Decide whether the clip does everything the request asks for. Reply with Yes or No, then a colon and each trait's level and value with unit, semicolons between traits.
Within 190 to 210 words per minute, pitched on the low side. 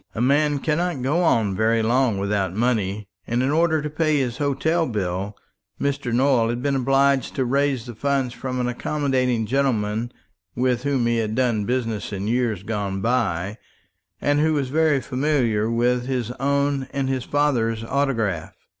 No: average, 165 wpm; low, 125 Hz